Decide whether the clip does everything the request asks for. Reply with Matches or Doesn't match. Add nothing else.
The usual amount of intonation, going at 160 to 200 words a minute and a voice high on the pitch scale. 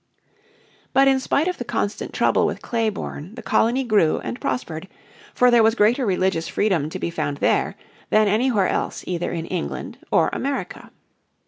Doesn't match